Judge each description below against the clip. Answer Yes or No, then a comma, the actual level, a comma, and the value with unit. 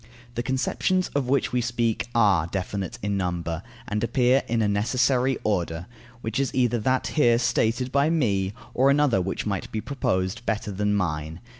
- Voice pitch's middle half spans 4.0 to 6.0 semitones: Yes, average, 4.7 semitones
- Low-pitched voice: Yes, low, 115 Hz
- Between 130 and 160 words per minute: No, average, 170 wpm